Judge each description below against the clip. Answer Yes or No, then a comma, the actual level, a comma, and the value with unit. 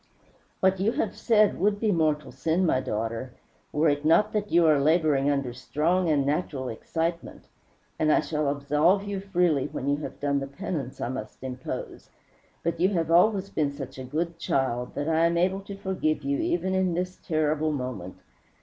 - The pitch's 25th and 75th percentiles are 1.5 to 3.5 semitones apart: No, average, 4.6 semitones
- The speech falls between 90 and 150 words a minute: No, average, 185 wpm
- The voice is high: No, medium, 155 Hz